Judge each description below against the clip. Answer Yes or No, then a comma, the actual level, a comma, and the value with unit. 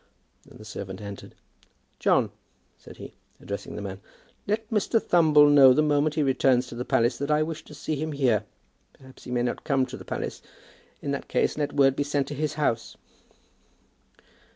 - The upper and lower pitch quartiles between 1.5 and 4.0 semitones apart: Yes, average, 3.6 semitones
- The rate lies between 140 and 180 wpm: No, average, 190 wpm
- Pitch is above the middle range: No, medium, 140 Hz